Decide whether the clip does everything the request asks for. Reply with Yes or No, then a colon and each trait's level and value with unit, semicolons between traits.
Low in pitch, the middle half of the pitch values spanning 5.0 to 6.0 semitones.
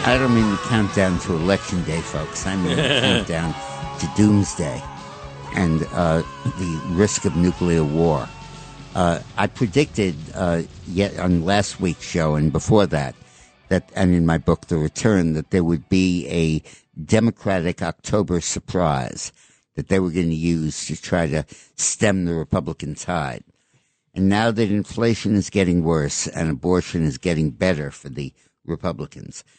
No: very low, 90 Hz; average, 3.8 semitones